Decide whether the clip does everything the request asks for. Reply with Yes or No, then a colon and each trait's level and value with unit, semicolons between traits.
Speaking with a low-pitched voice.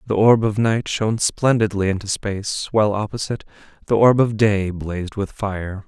Yes: low, 105 Hz